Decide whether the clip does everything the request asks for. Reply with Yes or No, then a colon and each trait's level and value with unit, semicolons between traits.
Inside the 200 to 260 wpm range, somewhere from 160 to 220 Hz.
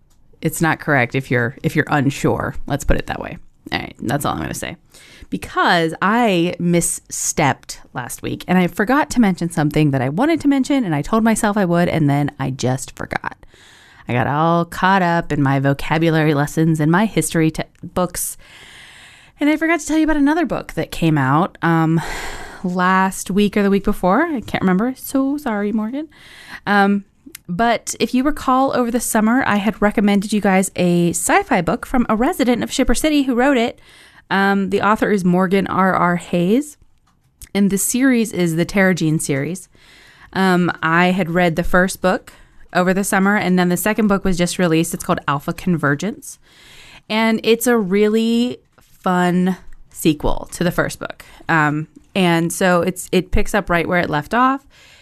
No: average, 185 wpm; medium, 185 Hz